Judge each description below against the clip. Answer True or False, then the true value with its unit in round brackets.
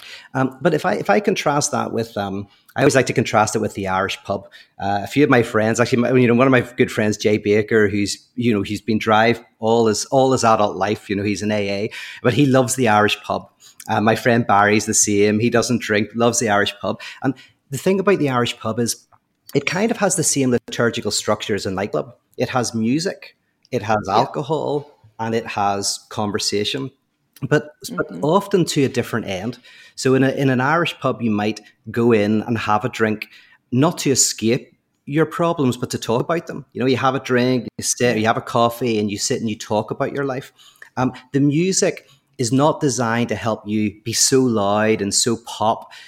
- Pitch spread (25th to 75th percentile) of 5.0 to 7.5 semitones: False (3.7 semitones)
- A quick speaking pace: True (220 wpm)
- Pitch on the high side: False (120 Hz)